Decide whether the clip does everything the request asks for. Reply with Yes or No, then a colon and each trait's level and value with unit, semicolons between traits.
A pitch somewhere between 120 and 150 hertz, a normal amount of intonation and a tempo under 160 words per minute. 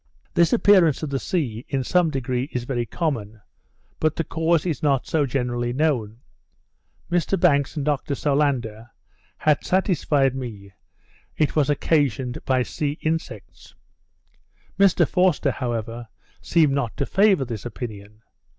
Yes: medium, 140 Hz; average, 4.8 semitones; average, 140 wpm